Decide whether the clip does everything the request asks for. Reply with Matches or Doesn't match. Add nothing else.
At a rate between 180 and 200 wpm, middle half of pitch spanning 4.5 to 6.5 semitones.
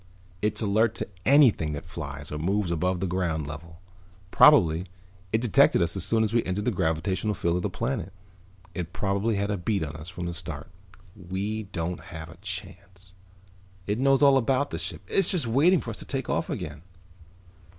Matches